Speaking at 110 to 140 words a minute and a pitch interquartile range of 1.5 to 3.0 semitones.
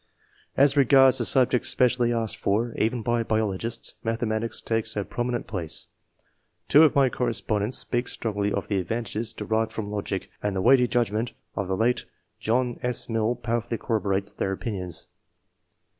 No: average, 155 wpm; average, 2.7 semitones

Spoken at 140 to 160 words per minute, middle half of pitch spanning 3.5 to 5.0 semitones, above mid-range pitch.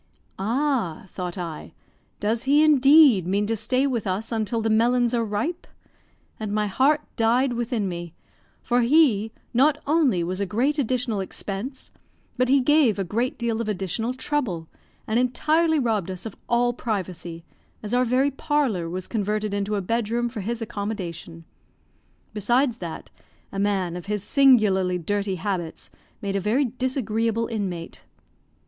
Yes: average, 155 wpm; average, 4.4 semitones; high, 225 Hz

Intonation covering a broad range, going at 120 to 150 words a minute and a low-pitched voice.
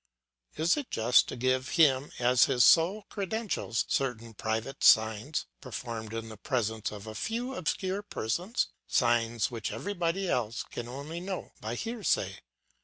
Yes: wide, 8.0 semitones; average, 145 wpm; low, 130 Hz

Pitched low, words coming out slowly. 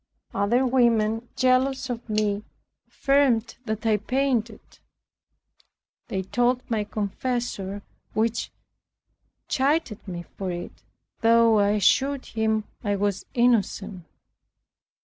No: high, 225 Hz; slow, 100 wpm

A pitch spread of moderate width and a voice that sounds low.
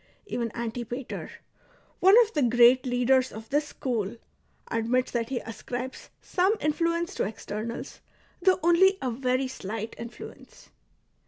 No: average, 4.6 semitones; very high, 250 Hz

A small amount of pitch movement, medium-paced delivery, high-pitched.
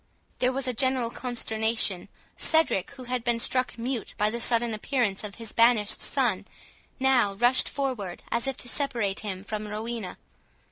No: average, 3.2 semitones; average, 160 wpm; high, 235 Hz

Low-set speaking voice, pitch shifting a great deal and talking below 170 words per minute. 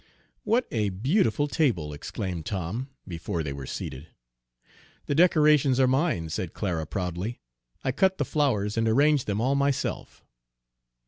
Yes: low, 115 Hz; wide, 8.3 semitones; average, 140 wpm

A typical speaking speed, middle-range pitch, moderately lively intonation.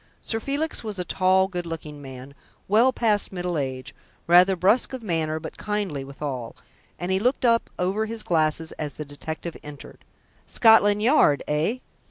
No: average, 165 wpm; medium, 180 Hz; wide, 5.9 semitones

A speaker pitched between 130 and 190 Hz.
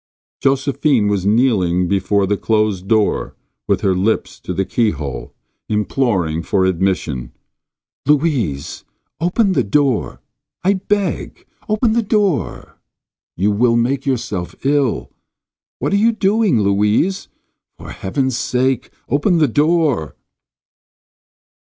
No: low, 120 Hz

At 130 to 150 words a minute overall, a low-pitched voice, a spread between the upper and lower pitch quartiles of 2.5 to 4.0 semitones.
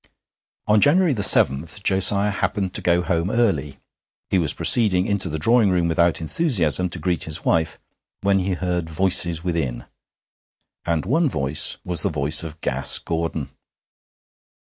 Yes: average, 145 wpm; very low, 90 Hz; average, 3.6 semitones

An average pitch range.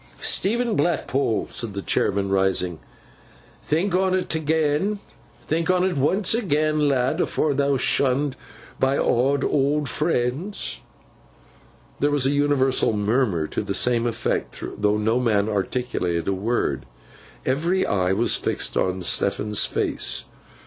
No: wide, 6.5 semitones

